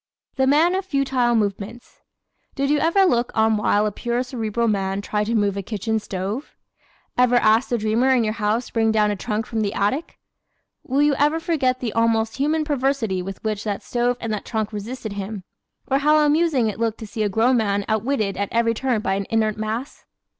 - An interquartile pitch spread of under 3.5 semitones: No, average, 3.8 semitones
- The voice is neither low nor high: No, high, 225 Hz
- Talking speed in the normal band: No, fast, 210 wpm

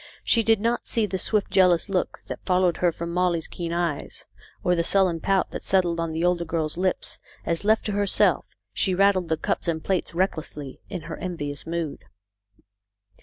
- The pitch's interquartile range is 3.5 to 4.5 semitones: No, narrow, 2.4 semitones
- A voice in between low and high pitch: Yes, medium, 180 Hz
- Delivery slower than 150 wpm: No, average, 185 wpm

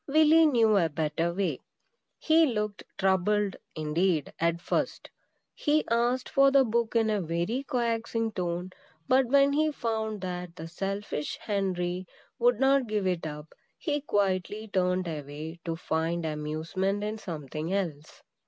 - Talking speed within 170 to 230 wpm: No, average, 145 wpm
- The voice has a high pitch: Yes, high, 195 Hz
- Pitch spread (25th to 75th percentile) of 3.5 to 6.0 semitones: Yes, wide, 5.5 semitones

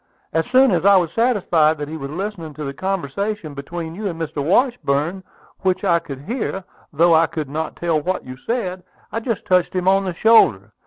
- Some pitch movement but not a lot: Yes, average, 4.3 semitones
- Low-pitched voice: No, medium, 170 Hz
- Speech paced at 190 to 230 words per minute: Yes, fast, 205 wpm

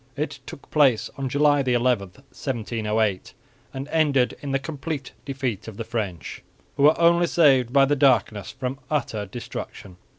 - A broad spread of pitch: No, average, 4.0 semitones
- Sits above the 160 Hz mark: No, low, 130 Hz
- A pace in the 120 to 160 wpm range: Yes, average, 155 wpm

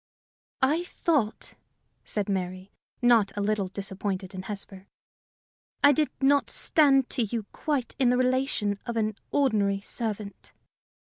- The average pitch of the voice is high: Yes, high, 215 Hz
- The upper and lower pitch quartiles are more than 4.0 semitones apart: Yes, average, 4.9 semitones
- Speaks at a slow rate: Yes, slow, 130 wpm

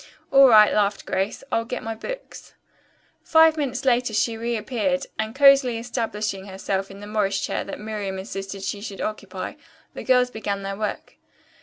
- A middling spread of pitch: Yes, average, 3.8 semitones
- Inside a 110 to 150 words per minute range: No, average, 165 wpm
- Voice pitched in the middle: No, high, 220 Hz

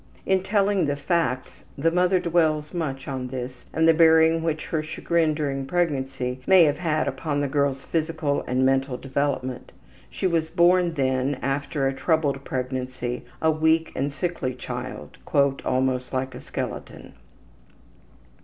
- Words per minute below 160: Yes, average, 145 wpm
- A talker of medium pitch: Yes, medium, 145 Hz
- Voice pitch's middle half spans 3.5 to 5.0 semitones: Yes, average, 3.8 semitones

